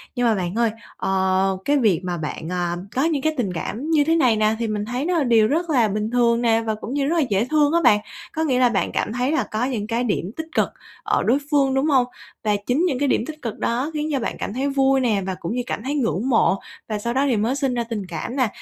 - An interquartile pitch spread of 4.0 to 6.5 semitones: Yes, average, 4.7 semitones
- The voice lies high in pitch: Yes, high, 240 Hz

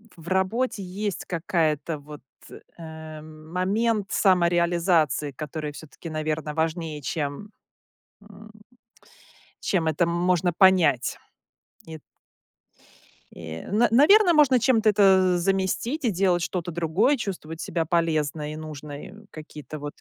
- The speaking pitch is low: No, medium, 170 Hz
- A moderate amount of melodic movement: Yes, average, 4.0 semitones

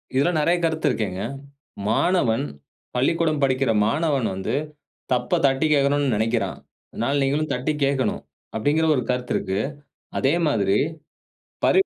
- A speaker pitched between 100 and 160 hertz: Yes, low, 135 Hz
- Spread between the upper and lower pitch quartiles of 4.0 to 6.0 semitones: Yes, average, 4.6 semitones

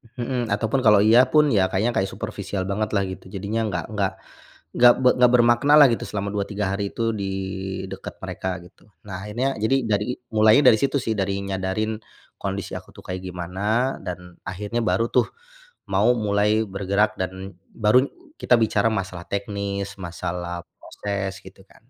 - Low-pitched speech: Yes, low, 100 Hz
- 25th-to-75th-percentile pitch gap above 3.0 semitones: No, average, 2.7 semitones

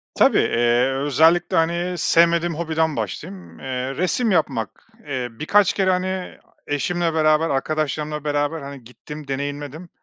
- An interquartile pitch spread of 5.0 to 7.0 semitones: No, average, 4.0 semitones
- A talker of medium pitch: Yes, medium, 155 Hz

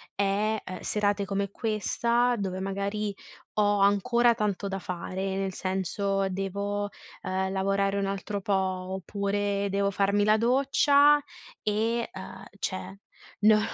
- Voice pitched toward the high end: Yes, high, 200 Hz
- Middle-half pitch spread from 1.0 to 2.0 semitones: Yes, narrow, 1.6 semitones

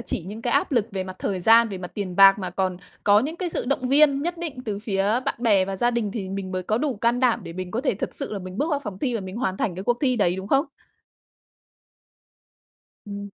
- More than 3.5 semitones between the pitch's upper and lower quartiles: Yes, average, 4.6 semitones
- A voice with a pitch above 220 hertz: No, high, 210 Hz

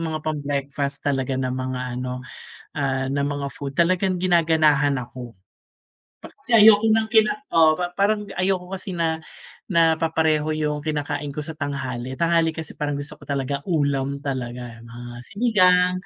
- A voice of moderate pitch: Yes, medium, 150 Hz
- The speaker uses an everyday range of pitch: Yes, average, 3.9 semitones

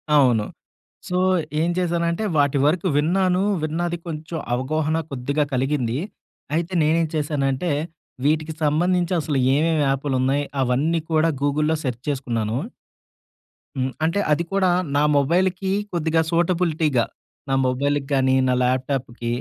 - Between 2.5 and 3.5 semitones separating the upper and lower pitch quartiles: No, average, 3.9 semitones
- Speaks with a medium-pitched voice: Yes, medium, 150 Hz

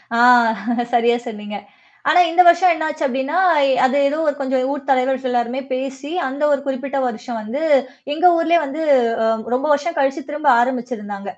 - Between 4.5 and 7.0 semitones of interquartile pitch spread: No, average, 3.2 semitones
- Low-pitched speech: No, very high, 270 Hz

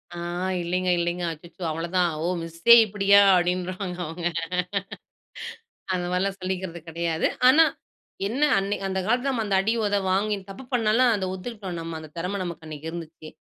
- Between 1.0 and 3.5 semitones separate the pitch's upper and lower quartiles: Yes, average, 3.0 semitones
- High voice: No, medium, 180 Hz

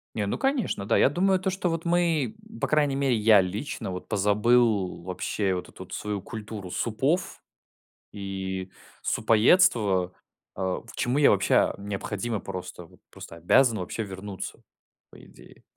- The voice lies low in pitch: Yes, low, 105 Hz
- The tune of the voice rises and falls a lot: Yes, wide, 6.2 semitones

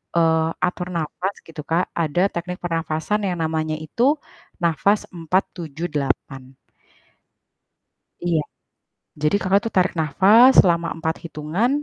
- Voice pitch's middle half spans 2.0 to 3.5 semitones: Yes, average, 2.8 semitones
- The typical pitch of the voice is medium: Yes, medium, 170 Hz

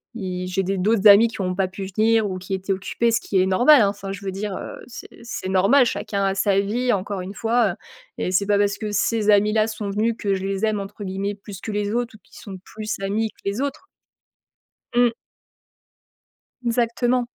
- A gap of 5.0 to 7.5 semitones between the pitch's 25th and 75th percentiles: No, narrow, 2.5 semitones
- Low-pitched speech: No, high, 205 Hz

